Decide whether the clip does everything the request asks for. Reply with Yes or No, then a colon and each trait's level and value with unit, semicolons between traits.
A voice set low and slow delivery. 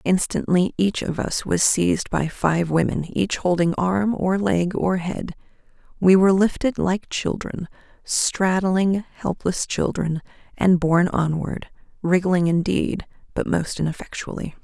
No: medium, 180 Hz; slow, 130 wpm